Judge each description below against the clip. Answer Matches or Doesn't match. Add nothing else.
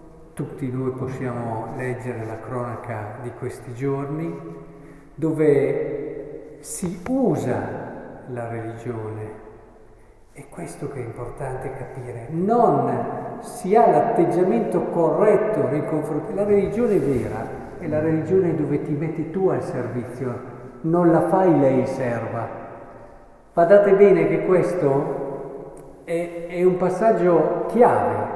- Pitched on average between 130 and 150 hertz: Matches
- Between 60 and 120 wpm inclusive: Matches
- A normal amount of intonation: Doesn't match